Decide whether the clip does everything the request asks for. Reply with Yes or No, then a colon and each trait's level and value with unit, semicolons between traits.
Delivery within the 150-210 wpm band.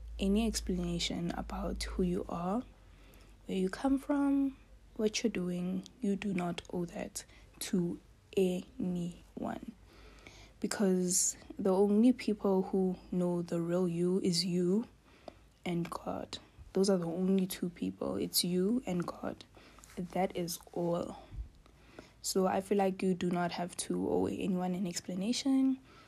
No: slow, 135 wpm